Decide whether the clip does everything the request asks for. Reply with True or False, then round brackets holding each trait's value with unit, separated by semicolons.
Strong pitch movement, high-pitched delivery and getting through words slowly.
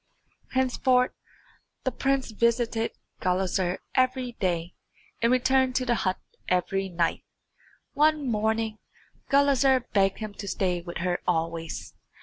True (5.9 semitones; 220 Hz; 120 wpm)